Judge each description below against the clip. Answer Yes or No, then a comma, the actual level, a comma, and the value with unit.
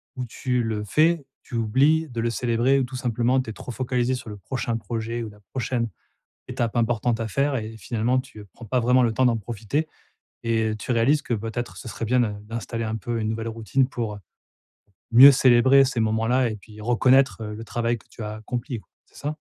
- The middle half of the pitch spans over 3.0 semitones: No, narrow, 2.4 semitones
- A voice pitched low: Yes, low, 120 Hz